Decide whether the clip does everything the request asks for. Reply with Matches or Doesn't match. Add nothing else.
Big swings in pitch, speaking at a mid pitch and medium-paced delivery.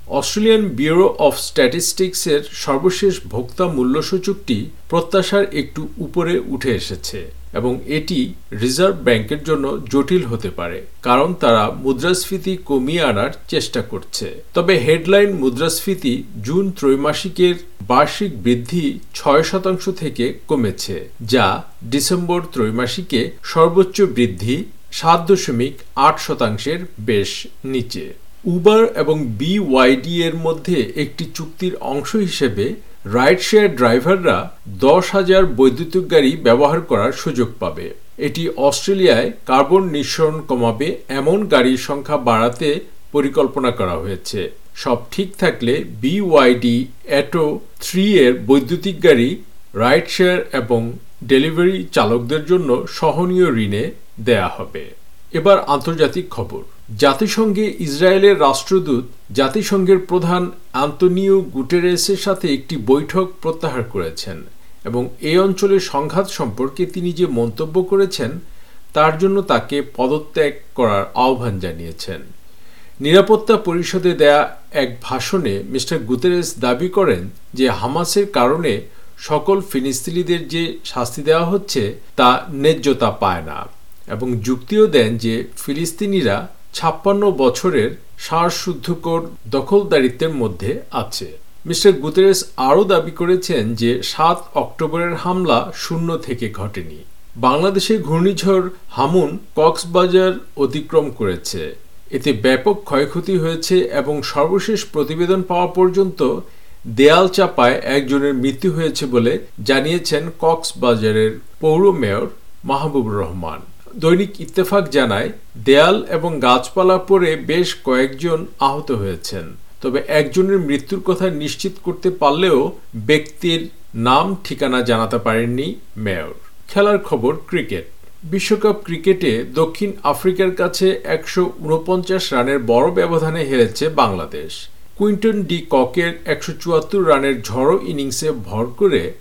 Matches